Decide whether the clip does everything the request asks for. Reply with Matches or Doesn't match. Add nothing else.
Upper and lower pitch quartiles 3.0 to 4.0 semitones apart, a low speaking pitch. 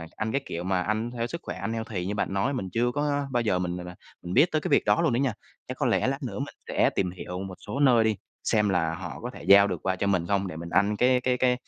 Doesn't match